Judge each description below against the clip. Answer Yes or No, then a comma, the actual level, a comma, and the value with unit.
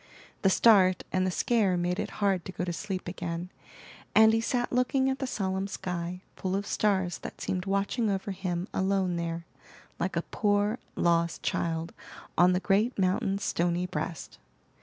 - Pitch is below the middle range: No, high, 190 Hz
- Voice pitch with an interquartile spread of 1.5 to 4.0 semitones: Yes, narrow, 2.6 semitones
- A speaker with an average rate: Yes, average, 170 wpm